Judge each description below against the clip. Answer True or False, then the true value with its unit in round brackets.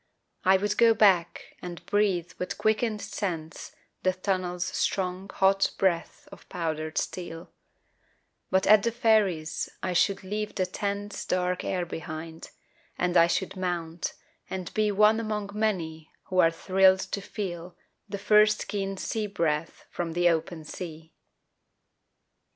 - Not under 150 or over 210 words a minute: False (140 wpm)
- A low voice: False (185 Hz)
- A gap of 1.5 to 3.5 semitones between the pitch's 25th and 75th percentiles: True (3.2 semitones)